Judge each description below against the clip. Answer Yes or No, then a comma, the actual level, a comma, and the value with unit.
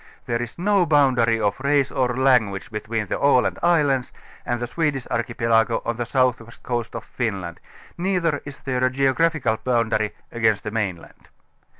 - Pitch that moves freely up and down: No, average, 3.5 semitones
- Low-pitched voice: Yes, low, 120 Hz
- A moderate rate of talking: Yes, average, 165 wpm